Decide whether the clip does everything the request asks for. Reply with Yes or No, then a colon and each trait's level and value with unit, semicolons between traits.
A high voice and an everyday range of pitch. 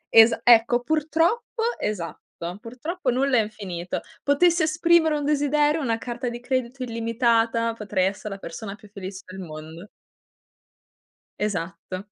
No: high, 235 Hz; wide, 6.1 semitones